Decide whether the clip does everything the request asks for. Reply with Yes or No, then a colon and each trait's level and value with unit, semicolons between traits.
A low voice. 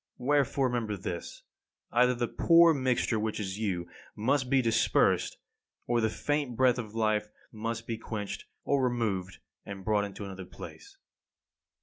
Yes: low, 115 Hz